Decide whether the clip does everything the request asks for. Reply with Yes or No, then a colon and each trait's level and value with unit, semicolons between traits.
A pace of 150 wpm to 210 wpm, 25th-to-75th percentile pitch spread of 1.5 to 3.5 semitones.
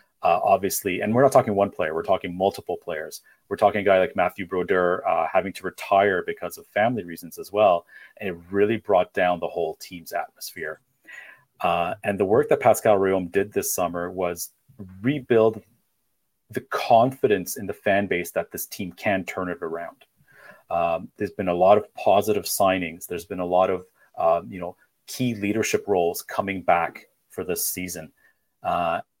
Yes: average, 180 wpm; narrow, 2.4 semitones